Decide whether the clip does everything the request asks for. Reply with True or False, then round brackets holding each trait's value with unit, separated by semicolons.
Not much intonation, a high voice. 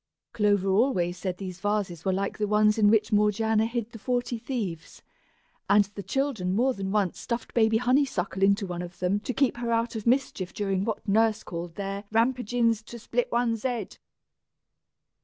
False (3.2 semitones; 210 Hz)